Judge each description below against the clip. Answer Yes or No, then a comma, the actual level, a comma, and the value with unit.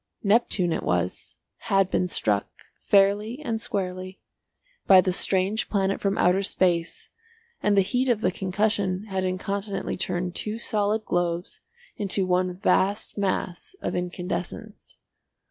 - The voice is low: No, high, 190 Hz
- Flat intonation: Yes, narrow, 2.1 semitones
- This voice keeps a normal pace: No, slow, 130 wpm